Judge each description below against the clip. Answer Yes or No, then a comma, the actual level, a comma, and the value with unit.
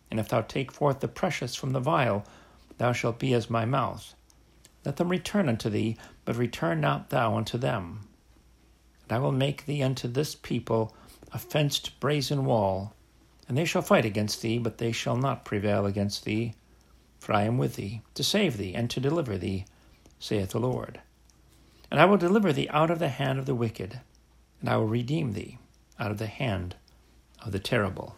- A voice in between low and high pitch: No, low, 115 Hz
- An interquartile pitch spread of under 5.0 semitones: No, average, 5.3 semitones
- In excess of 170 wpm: Yes, average, 195 wpm